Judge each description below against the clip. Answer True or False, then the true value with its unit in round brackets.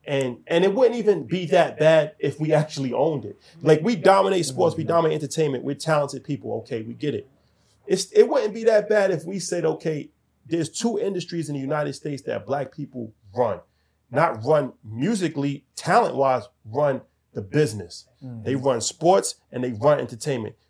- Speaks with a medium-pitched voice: True (150 Hz)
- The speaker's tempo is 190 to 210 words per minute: False (180 wpm)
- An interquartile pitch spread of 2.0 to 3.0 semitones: False (4.2 semitones)